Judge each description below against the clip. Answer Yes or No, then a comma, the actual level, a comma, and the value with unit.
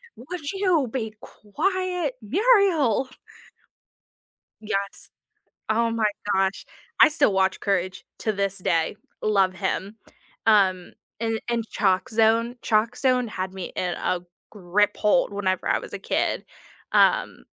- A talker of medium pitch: No, high, 215 Hz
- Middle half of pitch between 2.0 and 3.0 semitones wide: No, average, 5.0 semitones